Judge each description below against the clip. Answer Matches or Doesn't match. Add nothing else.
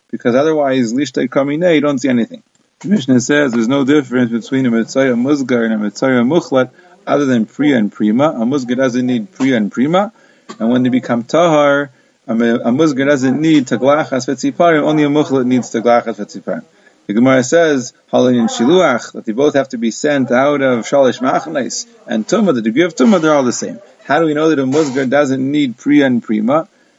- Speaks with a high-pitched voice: Doesn't match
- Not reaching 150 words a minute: Doesn't match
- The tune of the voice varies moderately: Matches